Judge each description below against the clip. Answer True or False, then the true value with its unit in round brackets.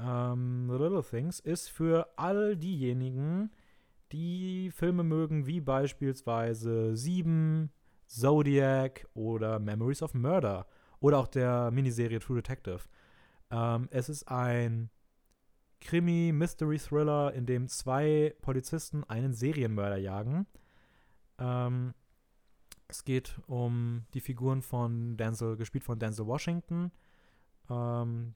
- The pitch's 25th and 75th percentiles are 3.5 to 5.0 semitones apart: True (4.7 semitones)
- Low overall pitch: True (130 Hz)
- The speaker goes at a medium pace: False (105 wpm)